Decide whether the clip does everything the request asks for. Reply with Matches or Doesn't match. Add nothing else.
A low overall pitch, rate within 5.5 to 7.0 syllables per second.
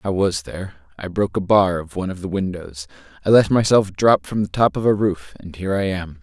Matches